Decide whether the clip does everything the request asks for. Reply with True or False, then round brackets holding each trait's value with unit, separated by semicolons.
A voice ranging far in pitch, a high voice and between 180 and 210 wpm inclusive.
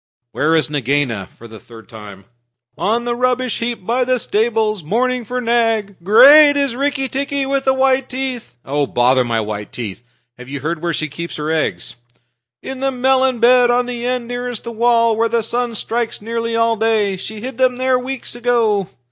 True (7.0 semitones; 230 Hz; 190 wpm)